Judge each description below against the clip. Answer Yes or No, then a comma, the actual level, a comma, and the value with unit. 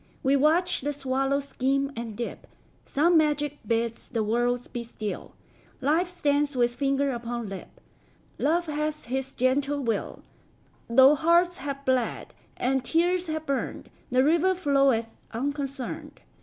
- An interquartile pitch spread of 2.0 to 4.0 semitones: Yes, average, 3.5 semitones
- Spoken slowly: Yes, slow, 115 wpm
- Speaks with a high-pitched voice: Yes, very high, 275 Hz